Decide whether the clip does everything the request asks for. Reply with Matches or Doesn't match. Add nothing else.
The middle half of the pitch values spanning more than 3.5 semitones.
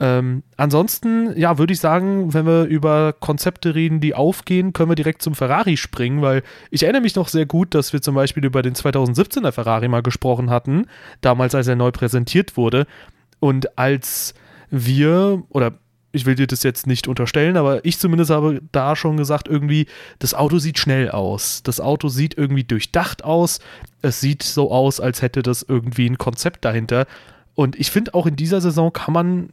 Matches